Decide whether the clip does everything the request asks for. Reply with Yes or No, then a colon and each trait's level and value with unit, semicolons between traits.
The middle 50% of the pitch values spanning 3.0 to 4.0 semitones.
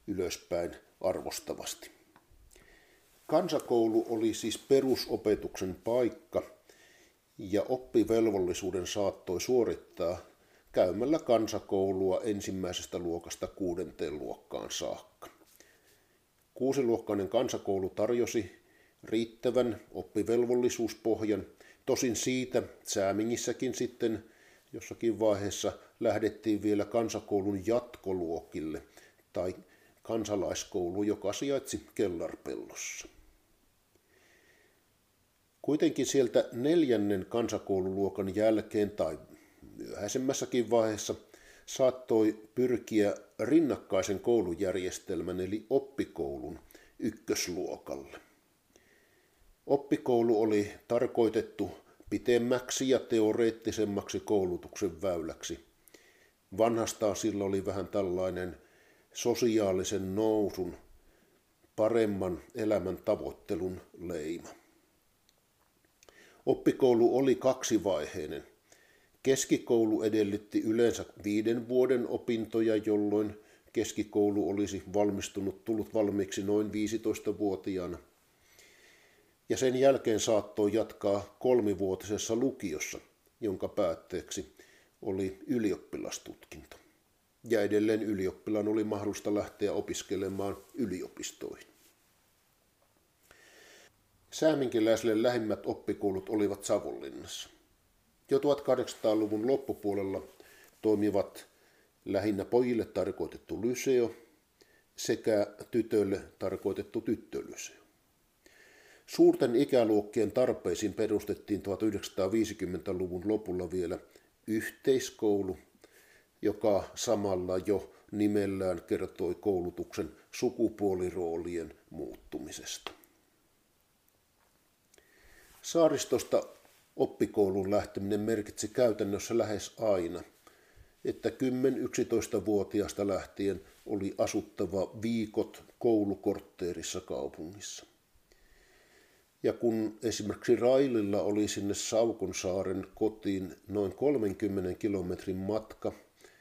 Yes: average, 3.3 semitones